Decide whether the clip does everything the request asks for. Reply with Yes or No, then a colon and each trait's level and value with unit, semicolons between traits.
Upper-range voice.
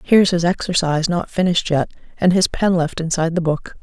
No: medium, 170 Hz